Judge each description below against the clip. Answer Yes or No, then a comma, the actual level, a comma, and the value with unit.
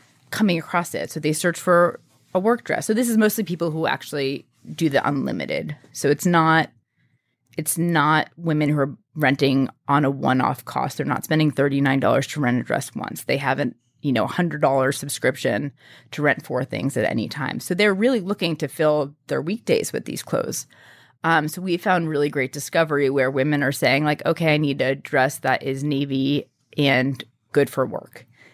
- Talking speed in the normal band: Yes, average, 195 wpm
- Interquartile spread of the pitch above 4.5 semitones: No, average, 3.7 semitones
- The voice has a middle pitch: Yes, medium, 150 Hz